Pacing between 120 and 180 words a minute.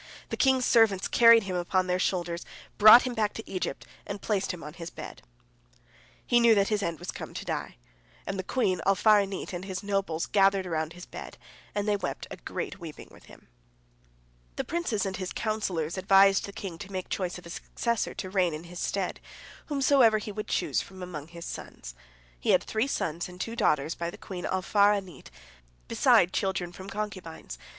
No: average, 190 wpm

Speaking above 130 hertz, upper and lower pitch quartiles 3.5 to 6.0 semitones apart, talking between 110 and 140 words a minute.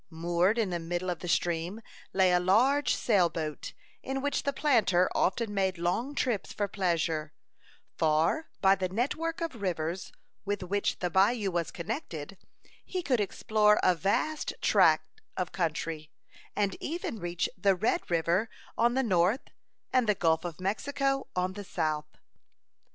No: high, 190 Hz; average, 5.0 semitones; average, 155 wpm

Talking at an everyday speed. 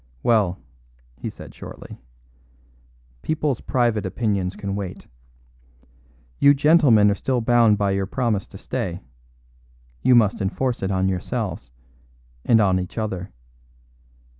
No: slow, 120 wpm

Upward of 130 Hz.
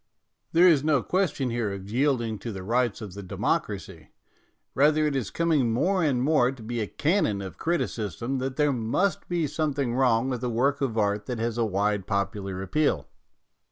No: low, 125 Hz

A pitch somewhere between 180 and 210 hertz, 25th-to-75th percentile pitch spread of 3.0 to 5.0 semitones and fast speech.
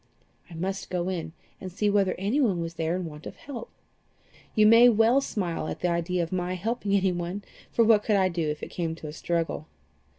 Yes: medium, 185 Hz; average, 3.6 semitones; fast, 210 wpm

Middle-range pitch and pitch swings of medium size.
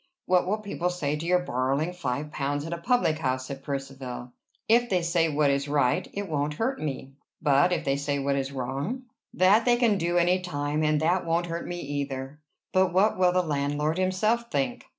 Yes: medium, 155 Hz; average, 4.6 semitones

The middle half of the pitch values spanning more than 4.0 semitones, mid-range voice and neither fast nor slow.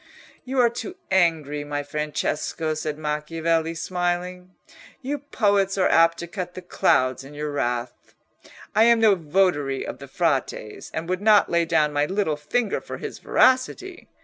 Yes: average, 4.6 semitones; medium, 165 Hz; average, 160 wpm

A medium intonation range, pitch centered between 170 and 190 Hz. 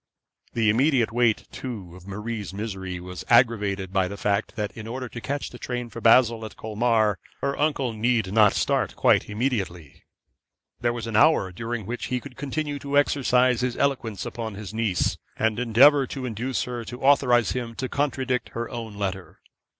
No: average, 3.3 semitones; low, 115 Hz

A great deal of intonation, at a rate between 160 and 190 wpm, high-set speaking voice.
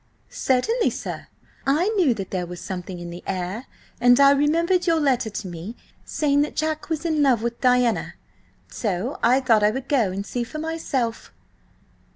Yes: wide, 6.4 semitones; average, 185 wpm; very high, 250 Hz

